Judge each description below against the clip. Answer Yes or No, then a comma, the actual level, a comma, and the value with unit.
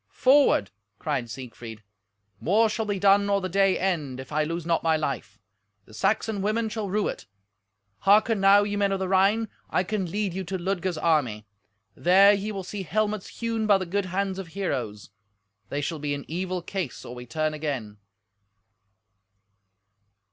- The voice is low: No, medium, 185 Hz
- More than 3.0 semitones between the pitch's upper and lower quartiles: Yes, average, 4.9 semitones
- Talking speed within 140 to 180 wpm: Yes, average, 175 wpm